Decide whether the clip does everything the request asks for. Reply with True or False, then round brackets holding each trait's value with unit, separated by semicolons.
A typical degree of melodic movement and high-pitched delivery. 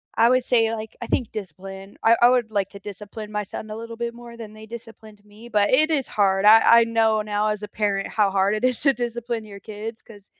False (2.1 semitones; 220 Hz)